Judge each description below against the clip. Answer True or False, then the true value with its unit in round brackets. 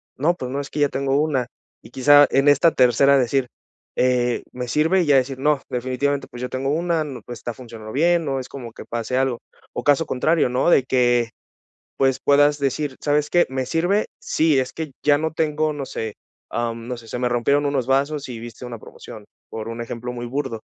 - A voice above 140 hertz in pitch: False (135 Hz)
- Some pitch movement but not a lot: True (3.0 semitones)